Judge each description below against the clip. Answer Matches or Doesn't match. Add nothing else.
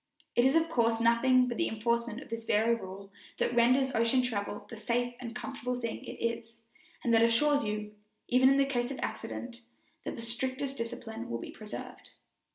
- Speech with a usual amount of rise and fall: Doesn't match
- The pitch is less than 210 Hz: Doesn't match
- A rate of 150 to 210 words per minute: Matches